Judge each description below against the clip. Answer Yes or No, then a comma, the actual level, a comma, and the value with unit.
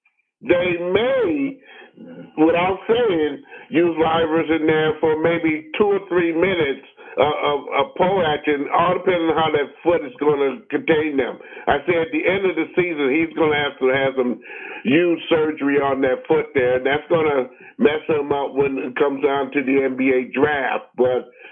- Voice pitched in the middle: Yes, medium, 160 Hz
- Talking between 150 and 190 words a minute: Yes, average, 180 wpm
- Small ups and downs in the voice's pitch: No, average, 3.8 semitones